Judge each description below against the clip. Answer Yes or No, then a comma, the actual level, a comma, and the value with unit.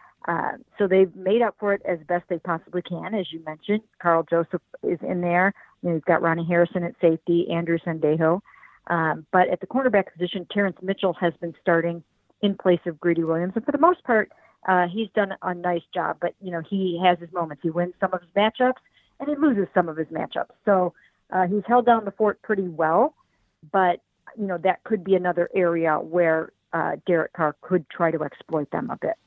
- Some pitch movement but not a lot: Yes, average, 3.0 semitones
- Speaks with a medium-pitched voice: Yes, medium, 180 Hz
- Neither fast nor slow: No, fast, 215 wpm